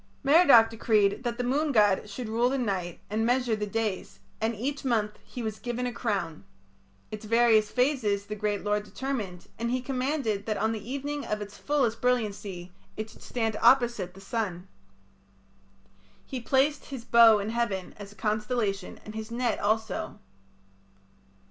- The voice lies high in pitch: Yes, high, 225 Hz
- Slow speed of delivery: No, average, 165 wpm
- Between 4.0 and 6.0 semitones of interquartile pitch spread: No, average, 3.2 semitones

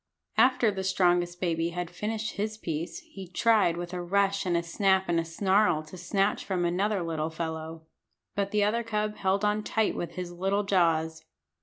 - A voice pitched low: No, medium, 185 Hz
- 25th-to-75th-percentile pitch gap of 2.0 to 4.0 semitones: Yes, average, 3.5 semitones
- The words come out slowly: No, average, 185 wpm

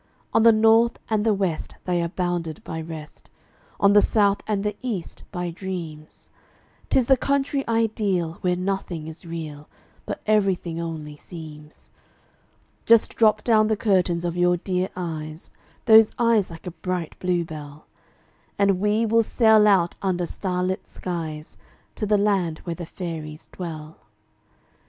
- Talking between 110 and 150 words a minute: Yes, average, 145 wpm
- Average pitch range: Yes, average, 4.3 semitones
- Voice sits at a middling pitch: Yes, medium, 180 Hz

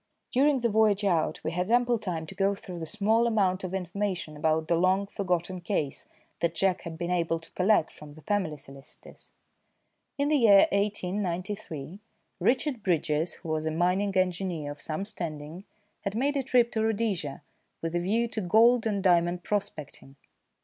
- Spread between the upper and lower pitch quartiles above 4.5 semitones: No, average, 4.2 semitones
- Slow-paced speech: No, average, 175 wpm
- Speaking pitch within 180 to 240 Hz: Yes, medium, 185 Hz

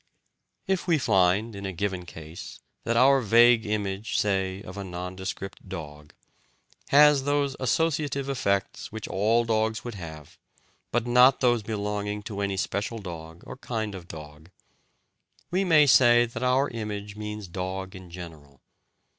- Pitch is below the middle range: Yes, low, 105 Hz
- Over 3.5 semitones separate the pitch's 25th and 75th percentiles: Yes, average, 4.5 semitones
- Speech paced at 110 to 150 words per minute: Yes, average, 145 wpm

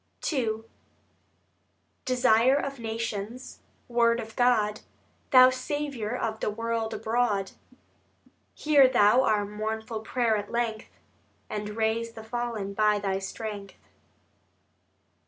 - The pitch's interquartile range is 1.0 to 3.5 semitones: Yes, narrow, 2.5 semitones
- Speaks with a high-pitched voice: Yes, high, 225 Hz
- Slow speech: Yes, slow, 105 wpm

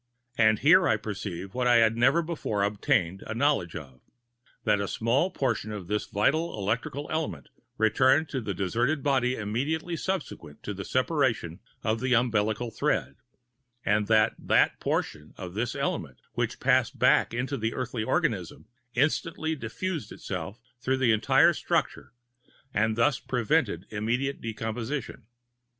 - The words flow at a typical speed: Yes, average, 145 wpm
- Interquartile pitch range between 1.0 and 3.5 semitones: No, average, 4.6 semitones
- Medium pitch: No, low, 115 Hz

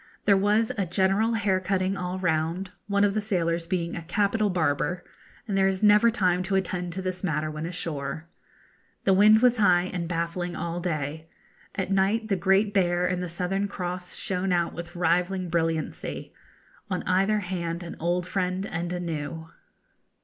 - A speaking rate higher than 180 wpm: No, average, 175 wpm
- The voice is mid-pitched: Yes, medium, 180 Hz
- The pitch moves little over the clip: Yes, narrow, 2.3 semitones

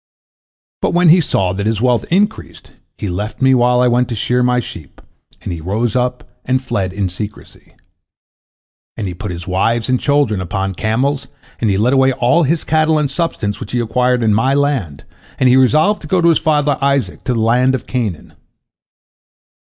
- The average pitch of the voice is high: No, low, 125 Hz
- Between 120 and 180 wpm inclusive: No, average, 195 wpm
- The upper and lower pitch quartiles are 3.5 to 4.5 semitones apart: No, average, 4.9 semitones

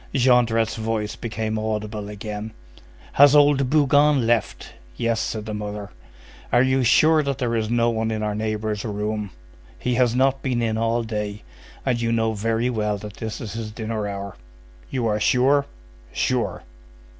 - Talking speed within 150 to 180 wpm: Yes, average, 165 wpm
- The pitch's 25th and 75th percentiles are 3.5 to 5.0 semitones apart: No, narrow, 2.5 semitones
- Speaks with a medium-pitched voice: No, low, 115 Hz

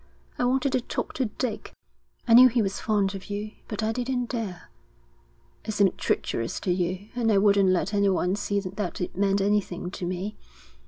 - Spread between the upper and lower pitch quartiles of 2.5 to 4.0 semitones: Yes, average, 3.0 semitones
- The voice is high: Yes, high, 205 Hz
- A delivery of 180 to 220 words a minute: Yes, average, 190 wpm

